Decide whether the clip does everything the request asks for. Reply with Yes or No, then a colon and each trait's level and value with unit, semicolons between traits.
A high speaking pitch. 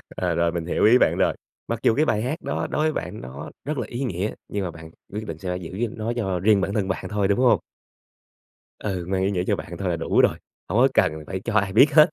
No: low, 100 Hz